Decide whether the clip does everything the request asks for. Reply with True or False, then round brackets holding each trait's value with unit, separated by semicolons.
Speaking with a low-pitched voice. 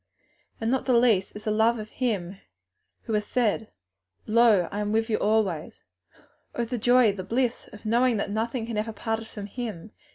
False (220 Hz)